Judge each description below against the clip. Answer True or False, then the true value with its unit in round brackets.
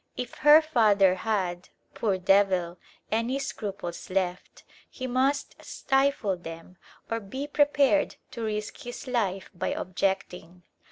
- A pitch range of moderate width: False (5.8 semitones)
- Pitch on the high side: True (210 Hz)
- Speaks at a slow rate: True (120 wpm)